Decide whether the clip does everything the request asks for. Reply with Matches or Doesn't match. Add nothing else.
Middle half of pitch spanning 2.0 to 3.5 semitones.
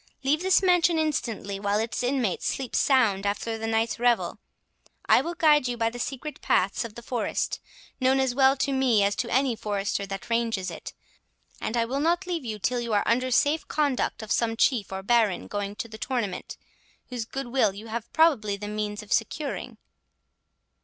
Doesn't match